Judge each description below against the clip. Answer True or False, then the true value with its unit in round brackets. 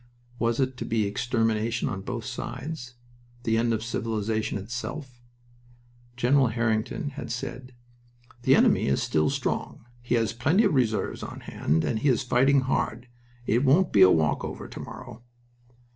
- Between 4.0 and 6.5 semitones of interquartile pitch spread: False (2.7 semitones)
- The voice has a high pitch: False (120 Hz)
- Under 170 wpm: True (160 wpm)